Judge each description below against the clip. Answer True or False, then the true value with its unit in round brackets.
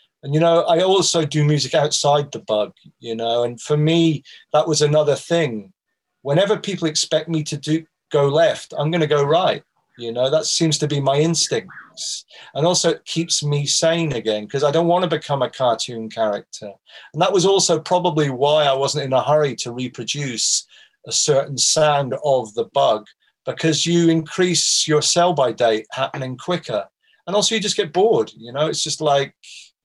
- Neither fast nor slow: False (190 wpm)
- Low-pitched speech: False (150 Hz)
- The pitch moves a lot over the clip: False (3.4 semitones)